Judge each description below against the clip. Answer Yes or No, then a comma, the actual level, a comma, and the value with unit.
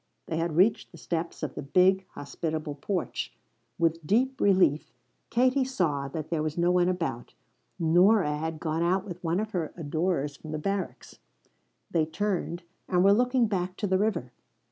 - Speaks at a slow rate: No, average, 170 wpm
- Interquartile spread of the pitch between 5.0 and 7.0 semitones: No, average, 3.9 semitones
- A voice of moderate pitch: Yes, medium, 175 Hz